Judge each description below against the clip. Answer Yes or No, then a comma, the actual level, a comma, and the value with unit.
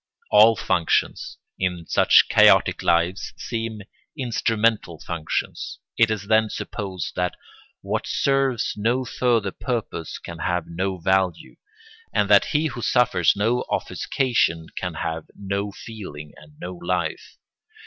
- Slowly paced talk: Yes, slow, 125 wpm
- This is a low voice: Yes, low, 100 Hz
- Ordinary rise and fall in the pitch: Yes, average, 4.9 semitones